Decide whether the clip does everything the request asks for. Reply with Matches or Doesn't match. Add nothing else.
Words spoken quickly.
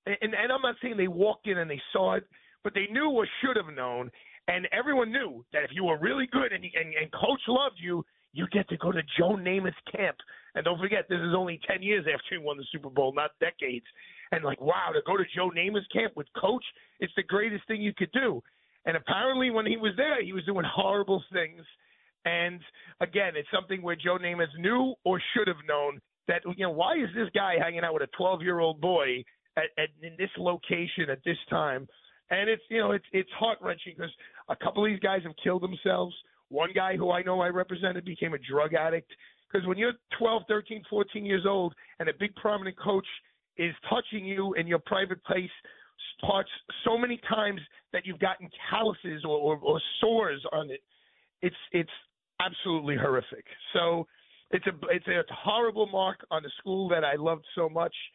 Matches